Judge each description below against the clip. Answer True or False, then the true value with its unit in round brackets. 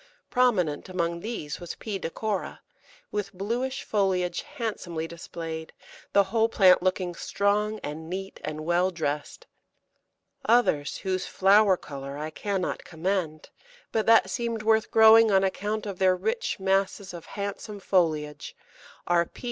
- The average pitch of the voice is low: False (190 Hz)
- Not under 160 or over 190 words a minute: False (135 wpm)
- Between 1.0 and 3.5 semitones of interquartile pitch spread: False (3.9 semitones)